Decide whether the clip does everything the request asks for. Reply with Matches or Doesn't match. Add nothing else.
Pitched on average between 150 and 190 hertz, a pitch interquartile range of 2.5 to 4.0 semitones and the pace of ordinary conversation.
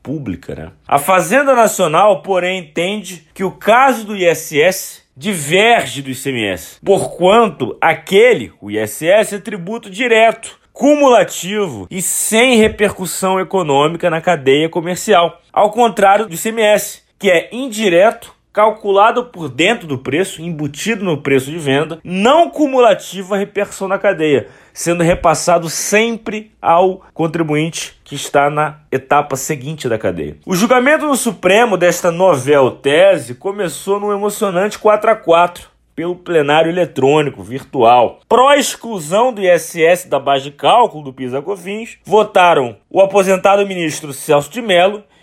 Doesn't match